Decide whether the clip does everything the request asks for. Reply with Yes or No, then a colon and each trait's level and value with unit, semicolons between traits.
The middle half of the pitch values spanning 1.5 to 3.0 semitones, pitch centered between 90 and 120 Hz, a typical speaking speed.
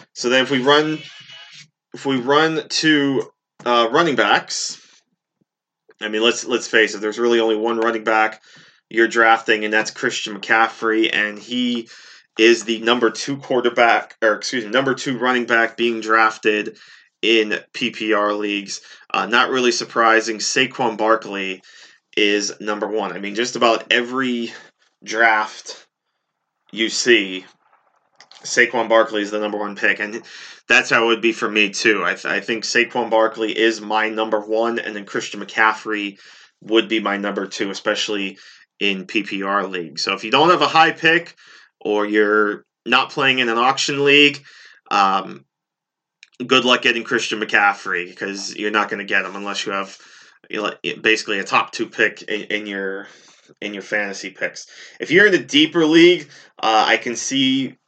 Yes: average, 2.7 semitones; low, 115 Hz; average, 165 wpm